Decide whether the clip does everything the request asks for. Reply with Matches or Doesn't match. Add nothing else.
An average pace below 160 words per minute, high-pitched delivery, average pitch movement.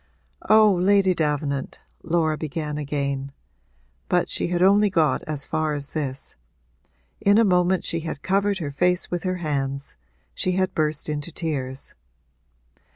Doesn't match